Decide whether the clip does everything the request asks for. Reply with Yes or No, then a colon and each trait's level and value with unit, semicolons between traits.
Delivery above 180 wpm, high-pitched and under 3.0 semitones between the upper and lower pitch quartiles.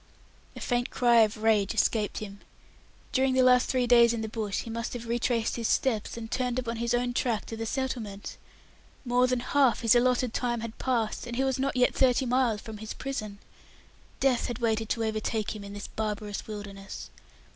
Yes: average, 200 wpm; high, 235 Hz; narrow, 2.4 semitones